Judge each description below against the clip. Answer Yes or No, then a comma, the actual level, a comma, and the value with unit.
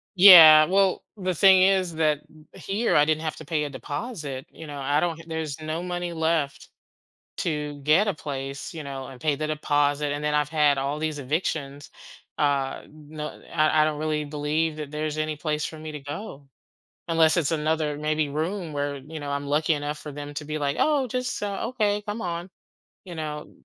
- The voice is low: No, medium, 155 Hz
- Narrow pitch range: Yes, narrow, 2.1 semitones